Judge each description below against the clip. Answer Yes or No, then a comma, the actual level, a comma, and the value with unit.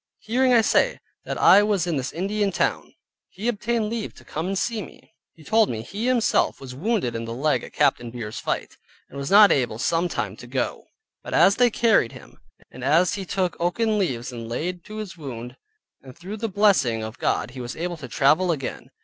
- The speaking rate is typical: No, fast, 215 wpm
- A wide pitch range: Yes, wide, 8.6 semitones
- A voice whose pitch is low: No, medium, 175 Hz